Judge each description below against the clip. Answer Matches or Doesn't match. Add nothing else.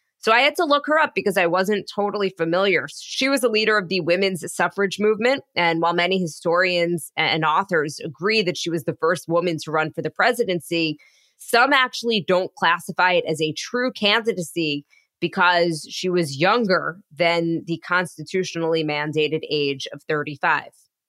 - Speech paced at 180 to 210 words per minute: Doesn't match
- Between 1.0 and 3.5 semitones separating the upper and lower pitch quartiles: Doesn't match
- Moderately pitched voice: Matches